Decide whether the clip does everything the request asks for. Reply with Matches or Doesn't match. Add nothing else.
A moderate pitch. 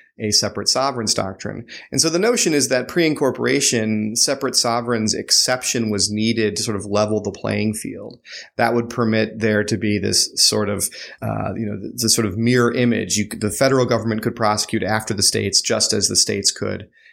Doesn't match